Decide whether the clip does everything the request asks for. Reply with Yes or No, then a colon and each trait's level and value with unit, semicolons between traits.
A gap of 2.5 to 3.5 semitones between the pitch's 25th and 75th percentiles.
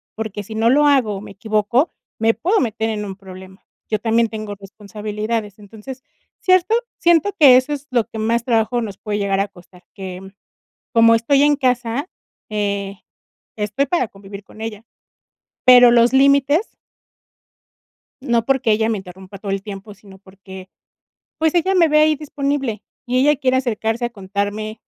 No: average, 4.4 semitones